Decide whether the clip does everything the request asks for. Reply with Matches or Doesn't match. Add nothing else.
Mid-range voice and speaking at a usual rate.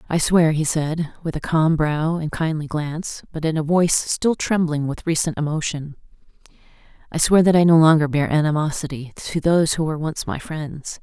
Matches